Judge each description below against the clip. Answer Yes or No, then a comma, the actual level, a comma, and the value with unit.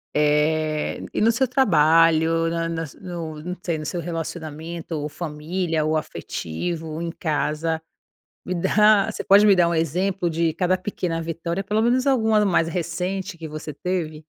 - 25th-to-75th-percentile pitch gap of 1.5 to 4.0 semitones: Yes, average, 2.7 semitones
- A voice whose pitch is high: No, medium, 165 Hz